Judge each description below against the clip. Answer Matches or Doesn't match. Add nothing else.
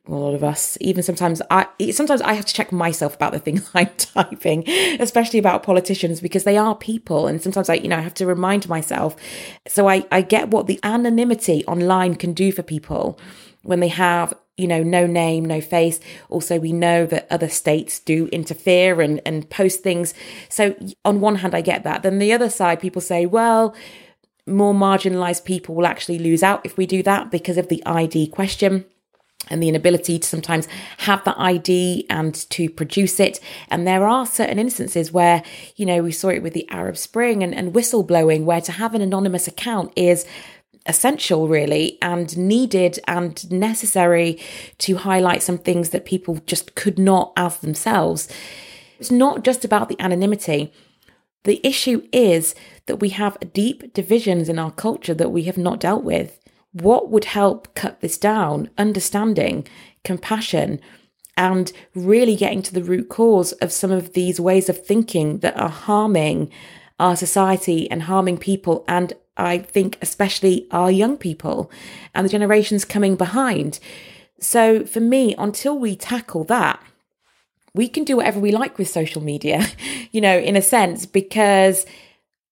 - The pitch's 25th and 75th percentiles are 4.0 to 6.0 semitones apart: Doesn't match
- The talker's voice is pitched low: Doesn't match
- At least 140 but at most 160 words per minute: Doesn't match